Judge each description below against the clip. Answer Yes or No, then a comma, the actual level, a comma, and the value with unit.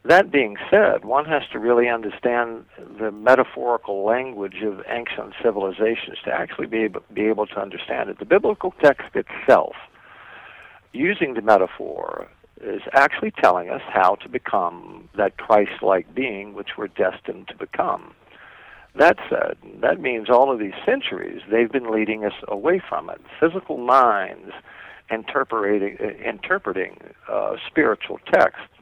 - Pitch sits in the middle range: No, low, 110 Hz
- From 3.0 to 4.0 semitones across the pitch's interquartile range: No, narrow, 2.6 semitones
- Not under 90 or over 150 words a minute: Yes, slow, 135 wpm